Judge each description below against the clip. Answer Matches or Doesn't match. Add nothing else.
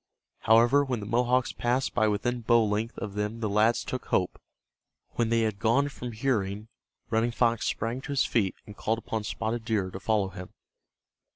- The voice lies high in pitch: Doesn't match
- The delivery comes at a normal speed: Matches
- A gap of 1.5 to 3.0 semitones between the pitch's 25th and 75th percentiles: Matches